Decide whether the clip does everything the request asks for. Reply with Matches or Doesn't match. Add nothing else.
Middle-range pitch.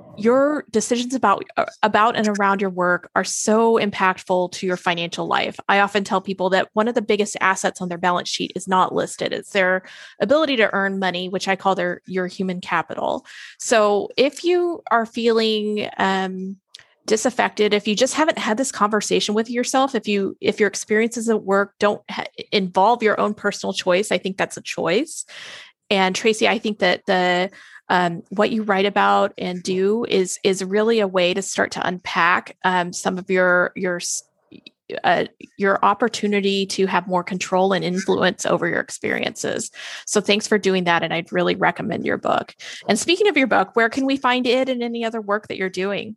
Doesn't match